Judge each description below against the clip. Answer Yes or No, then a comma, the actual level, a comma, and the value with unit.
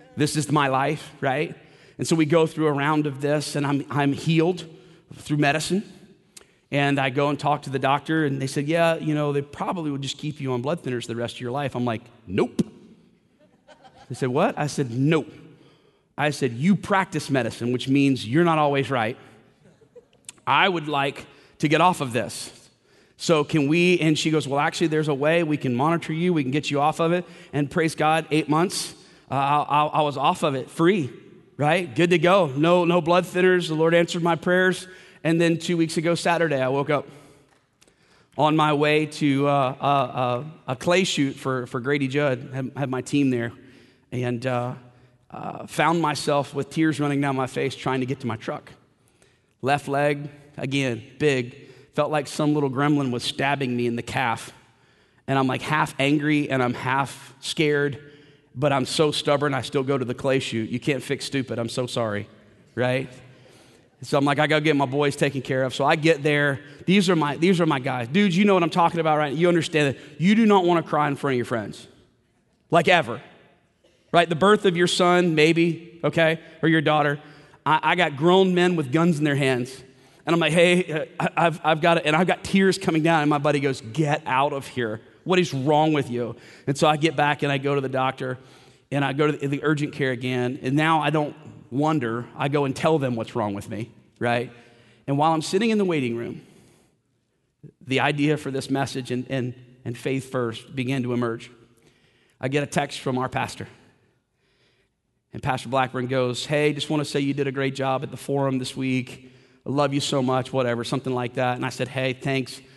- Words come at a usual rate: No, fast, 215 wpm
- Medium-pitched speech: Yes, medium, 145 Hz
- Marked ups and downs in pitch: No, average, 3.4 semitones